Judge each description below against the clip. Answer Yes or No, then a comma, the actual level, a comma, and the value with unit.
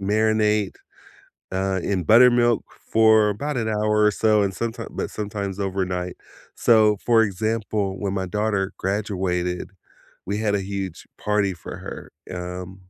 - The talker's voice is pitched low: Yes, low, 105 Hz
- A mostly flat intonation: Yes, narrow, 2.3 semitones